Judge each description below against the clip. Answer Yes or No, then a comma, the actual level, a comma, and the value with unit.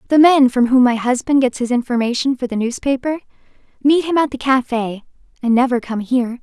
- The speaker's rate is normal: Yes, average, 195 wpm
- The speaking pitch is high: Yes, very high, 255 Hz